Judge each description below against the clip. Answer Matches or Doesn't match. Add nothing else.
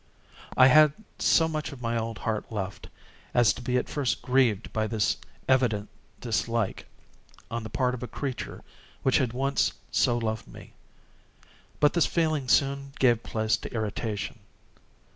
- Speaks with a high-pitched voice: Doesn't match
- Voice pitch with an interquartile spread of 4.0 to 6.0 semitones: Doesn't match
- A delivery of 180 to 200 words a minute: Doesn't match